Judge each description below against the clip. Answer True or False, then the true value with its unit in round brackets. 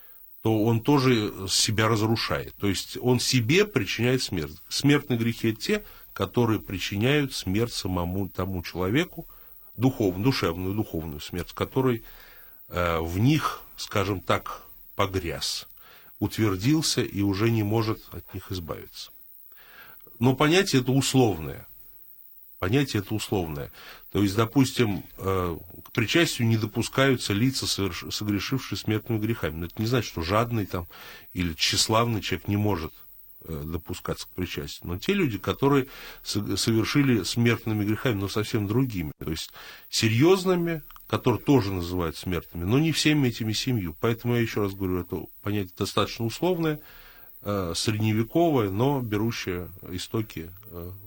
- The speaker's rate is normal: True (125 wpm)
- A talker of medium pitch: False (110 Hz)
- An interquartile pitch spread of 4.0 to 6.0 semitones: True (5.0 semitones)